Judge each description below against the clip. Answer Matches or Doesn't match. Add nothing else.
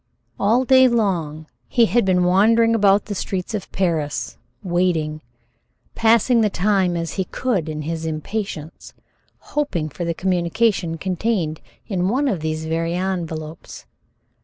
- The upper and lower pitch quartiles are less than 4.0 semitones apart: Doesn't match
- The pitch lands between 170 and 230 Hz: Matches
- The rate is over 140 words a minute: Doesn't match